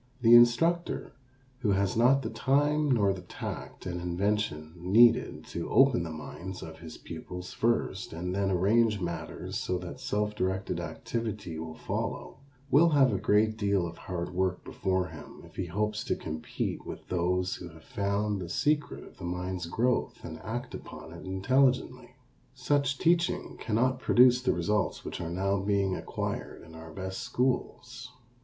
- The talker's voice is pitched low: Yes, low, 100 Hz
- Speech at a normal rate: Yes, average, 165 wpm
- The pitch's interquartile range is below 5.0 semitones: No, wide, 5.4 semitones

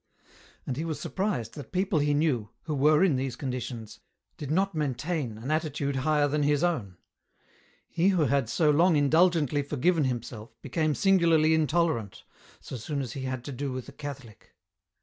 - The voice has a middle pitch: Yes, medium, 145 Hz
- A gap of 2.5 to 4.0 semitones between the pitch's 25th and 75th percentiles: Yes, average, 3.7 semitones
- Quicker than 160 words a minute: Yes, average, 170 wpm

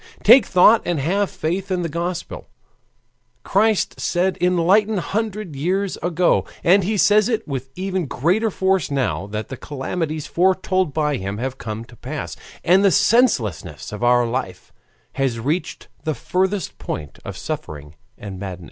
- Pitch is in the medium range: Yes, medium, 175 Hz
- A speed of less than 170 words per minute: Yes, average, 155 wpm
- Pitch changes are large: Yes, wide, 6.6 semitones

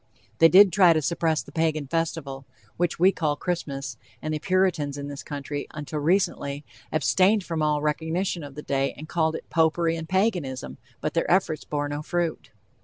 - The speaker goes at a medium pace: Yes, average, 180 wpm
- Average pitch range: Yes, average, 3.0 semitones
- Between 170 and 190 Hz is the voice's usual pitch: No, medium, 160 Hz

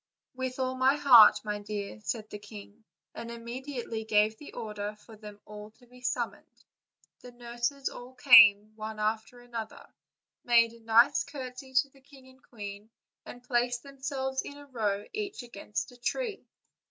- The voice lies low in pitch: No, high, 240 Hz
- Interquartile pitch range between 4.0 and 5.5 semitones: No, average, 3.4 semitones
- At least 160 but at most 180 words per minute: Yes, average, 165 wpm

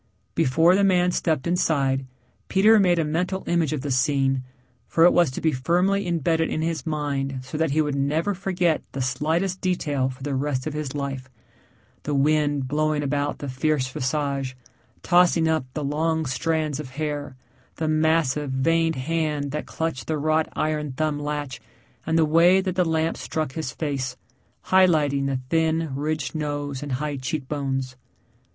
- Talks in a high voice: No, medium, 150 Hz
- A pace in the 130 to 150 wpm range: No, average, 170 wpm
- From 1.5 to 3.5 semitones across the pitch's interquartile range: Yes, average, 2.9 semitones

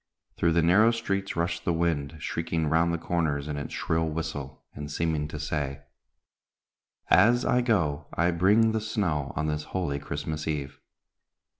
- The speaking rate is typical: Yes, average, 160 wpm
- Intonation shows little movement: No, average, 3.0 semitones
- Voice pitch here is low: Yes, very low, 80 Hz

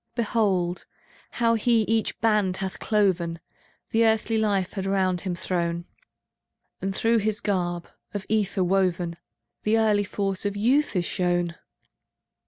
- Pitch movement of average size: Yes, average, 3.3 semitones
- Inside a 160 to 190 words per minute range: No, slow, 135 wpm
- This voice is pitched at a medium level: No, high, 195 Hz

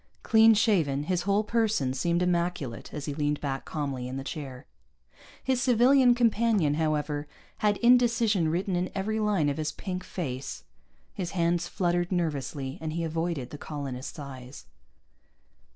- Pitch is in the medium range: Yes, medium, 170 Hz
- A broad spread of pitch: Yes, wide, 6.1 semitones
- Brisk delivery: No, average, 150 wpm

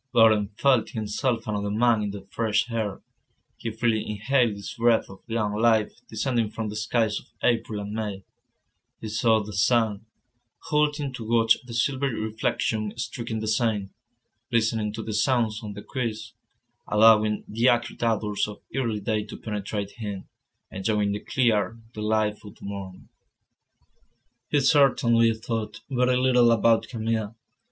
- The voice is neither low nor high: No, low, 110 Hz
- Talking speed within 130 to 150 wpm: Yes, average, 145 wpm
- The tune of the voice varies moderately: No, narrow, 2.0 semitones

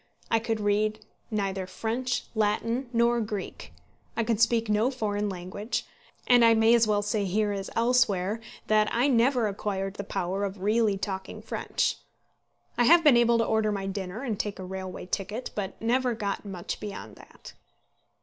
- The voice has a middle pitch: No, high, 215 Hz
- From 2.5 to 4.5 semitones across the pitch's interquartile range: Yes, average, 2.8 semitones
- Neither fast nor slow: Yes, average, 170 wpm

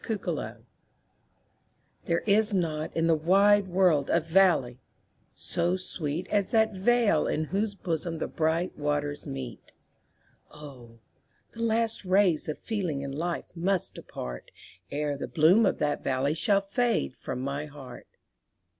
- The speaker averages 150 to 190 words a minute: No, slow, 135 wpm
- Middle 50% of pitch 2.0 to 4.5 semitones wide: No, average, 5.1 semitones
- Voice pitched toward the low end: No, medium, 165 Hz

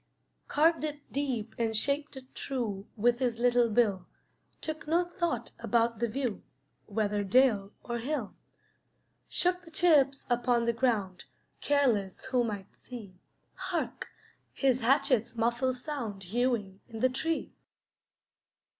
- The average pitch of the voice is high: Yes, high, 245 Hz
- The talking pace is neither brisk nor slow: No, slow, 130 wpm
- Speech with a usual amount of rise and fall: Yes, average, 4.1 semitones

